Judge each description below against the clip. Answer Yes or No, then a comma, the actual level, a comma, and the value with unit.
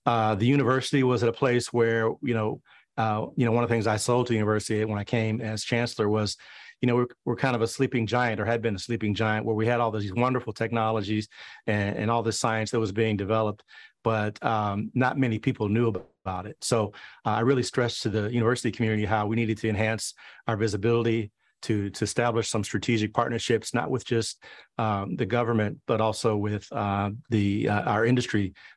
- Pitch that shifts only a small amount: Yes, narrow, 1.9 semitones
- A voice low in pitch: Yes, low, 115 Hz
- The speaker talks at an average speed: No, fast, 215 wpm